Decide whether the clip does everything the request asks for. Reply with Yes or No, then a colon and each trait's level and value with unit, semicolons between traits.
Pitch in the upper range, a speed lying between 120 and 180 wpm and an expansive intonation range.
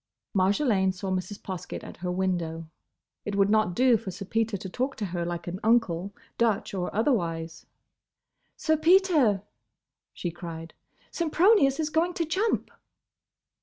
Yes: high, 200 Hz; average, 140 wpm; wide, 7.1 semitones